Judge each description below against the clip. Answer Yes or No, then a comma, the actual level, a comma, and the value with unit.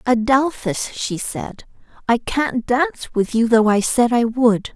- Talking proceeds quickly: No, average, 165 wpm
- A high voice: Yes, high, 235 Hz